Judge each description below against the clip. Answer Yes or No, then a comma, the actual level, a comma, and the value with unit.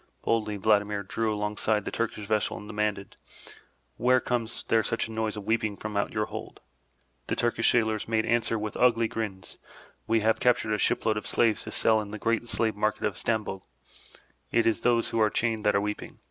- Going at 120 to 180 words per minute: No, average, 200 wpm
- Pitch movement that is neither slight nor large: No, narrow, 1.5 semitones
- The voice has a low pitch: Yes, low, 110 Hz